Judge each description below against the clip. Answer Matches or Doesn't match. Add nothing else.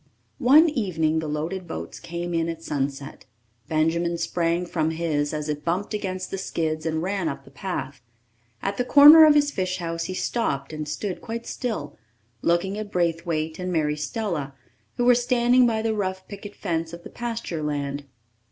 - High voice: Doesn't match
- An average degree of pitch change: Matches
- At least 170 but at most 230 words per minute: Matches